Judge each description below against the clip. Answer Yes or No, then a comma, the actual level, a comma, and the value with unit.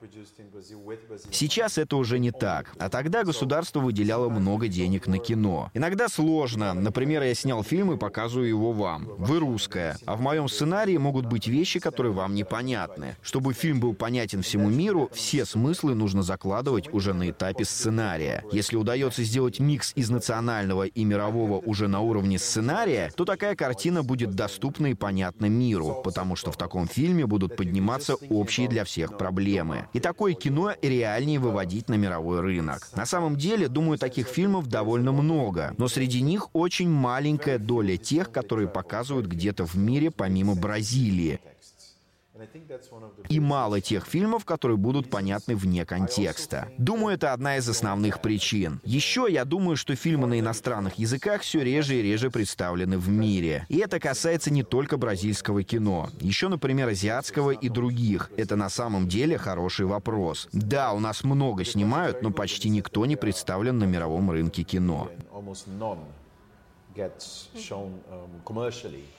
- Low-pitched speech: Yes, low, 115 Hz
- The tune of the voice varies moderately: No, wide, 5.7 semitones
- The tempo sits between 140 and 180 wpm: Yes, average, 150 wpm